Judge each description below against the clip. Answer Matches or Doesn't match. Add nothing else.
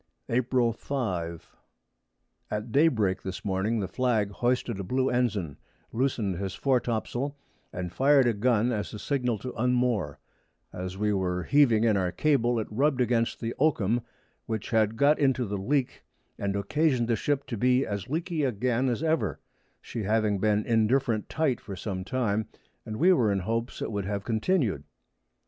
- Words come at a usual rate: Matches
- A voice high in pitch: Doesn't match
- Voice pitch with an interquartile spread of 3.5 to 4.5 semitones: Matches